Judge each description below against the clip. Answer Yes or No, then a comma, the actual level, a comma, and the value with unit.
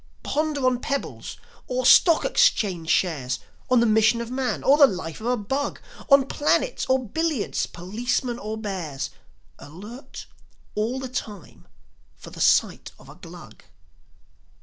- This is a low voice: No, high, 235 Hz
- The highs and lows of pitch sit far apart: Yes, wide, 5.7 semitones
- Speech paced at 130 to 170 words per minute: Yes, average, 145 wpm